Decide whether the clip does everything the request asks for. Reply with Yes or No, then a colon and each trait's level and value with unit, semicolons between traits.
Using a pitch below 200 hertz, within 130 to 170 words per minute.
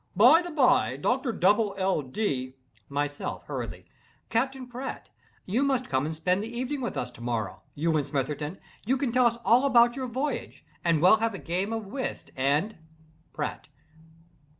No: high, 205 Hz; average, 165 wpm